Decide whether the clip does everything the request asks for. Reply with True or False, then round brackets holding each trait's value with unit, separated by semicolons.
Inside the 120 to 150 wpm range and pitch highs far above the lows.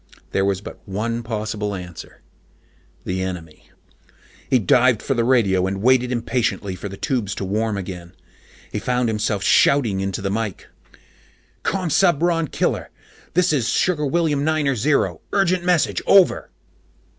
True (140 wpm; 6.5 semitones)